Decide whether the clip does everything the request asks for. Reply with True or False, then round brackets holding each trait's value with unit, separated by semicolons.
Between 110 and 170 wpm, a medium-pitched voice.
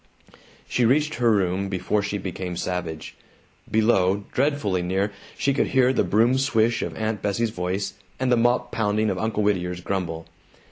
False (160 wpm; 105 Hz)